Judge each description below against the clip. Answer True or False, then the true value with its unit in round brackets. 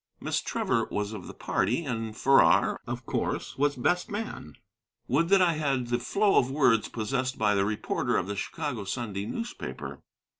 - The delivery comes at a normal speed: True (175 wpm)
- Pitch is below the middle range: True (125 Hz)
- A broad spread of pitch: True (6.3 semitones)